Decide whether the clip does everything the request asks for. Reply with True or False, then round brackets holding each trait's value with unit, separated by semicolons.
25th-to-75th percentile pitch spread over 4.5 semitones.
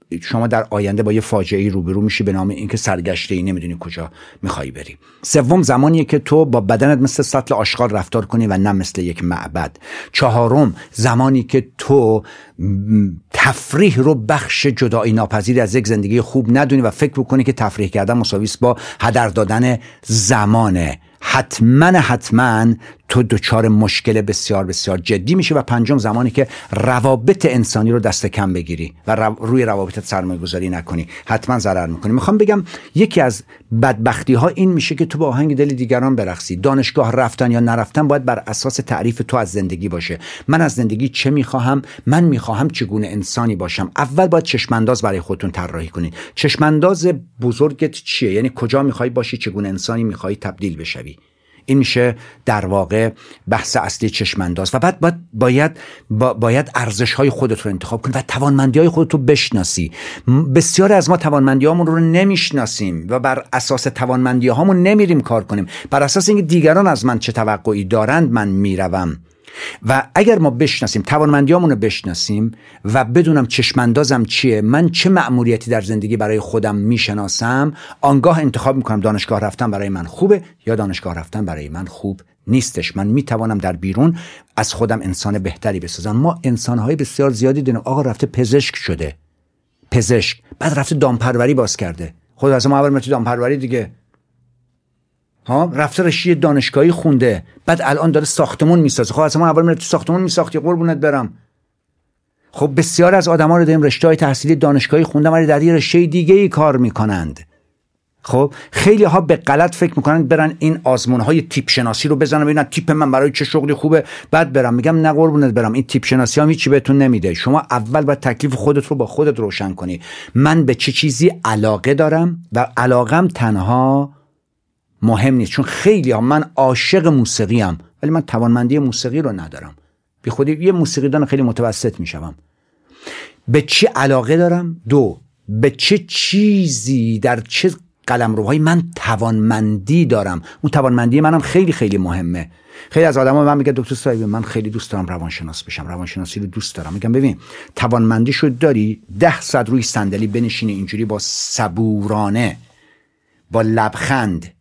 True (5.6 semitones)